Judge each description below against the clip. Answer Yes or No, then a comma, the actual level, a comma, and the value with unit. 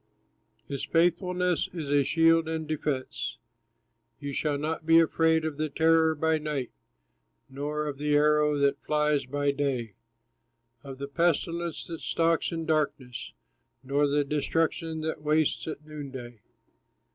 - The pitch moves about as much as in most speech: No, narrow, 2.3 semitones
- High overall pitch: No, medium, 150 Hz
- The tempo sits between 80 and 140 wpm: Yes, slow, 135 wpm